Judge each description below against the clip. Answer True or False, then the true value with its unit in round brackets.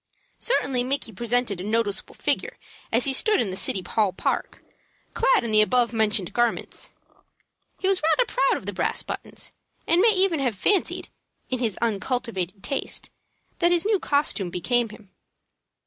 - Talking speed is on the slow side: False (165 wpm)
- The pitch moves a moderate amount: False (7.2 semitones)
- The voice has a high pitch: True (240 Hz)